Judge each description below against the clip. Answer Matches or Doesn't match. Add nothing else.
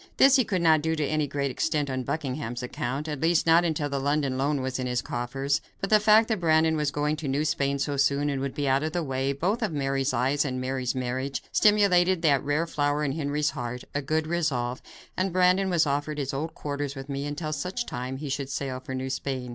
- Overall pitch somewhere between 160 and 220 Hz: Doesn't match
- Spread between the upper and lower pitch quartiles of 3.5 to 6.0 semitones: Doesn't match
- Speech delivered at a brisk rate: Matches